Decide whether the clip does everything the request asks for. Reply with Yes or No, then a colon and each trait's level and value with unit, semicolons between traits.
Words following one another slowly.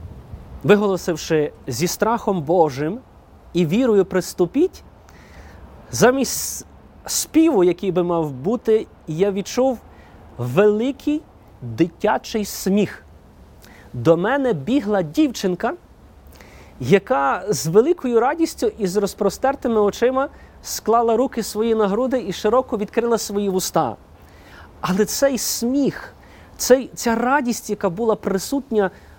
Yes: slow, 100 wpm